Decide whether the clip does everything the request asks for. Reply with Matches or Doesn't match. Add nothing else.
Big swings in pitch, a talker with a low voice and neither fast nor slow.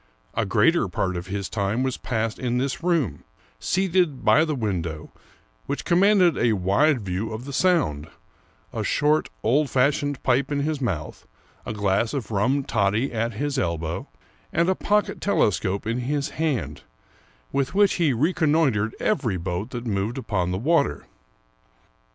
Matches